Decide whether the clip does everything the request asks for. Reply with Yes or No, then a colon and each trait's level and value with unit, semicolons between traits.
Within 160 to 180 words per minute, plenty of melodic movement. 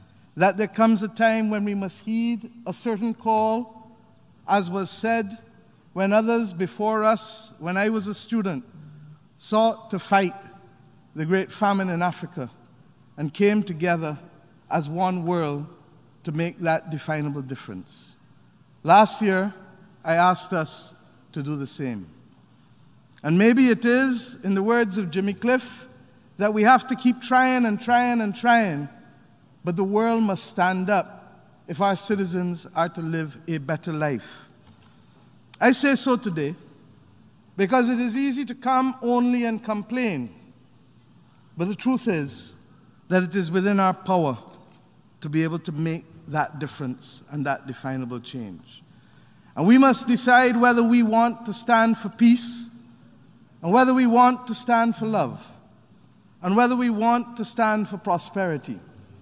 No: average, 150 wpm; wide, 6.3 semitones